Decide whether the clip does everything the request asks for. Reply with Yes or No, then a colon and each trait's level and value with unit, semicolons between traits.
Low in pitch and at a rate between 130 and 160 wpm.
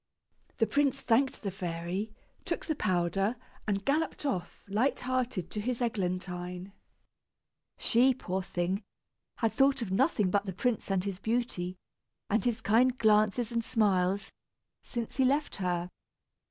No: high, 210 Hz; average, 140 wpm